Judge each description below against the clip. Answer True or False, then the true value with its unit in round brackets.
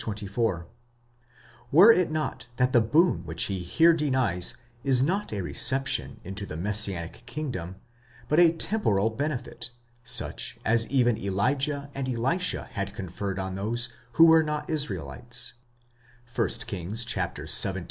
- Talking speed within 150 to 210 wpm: False (135 wpm)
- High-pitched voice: False (115 Hz)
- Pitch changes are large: True (7.0 semitones)